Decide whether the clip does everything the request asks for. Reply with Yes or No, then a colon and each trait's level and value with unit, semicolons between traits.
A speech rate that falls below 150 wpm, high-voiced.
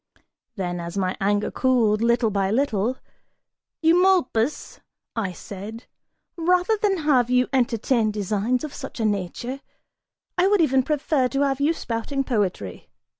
Yes: slow, 135 wpm; high, 245 Hz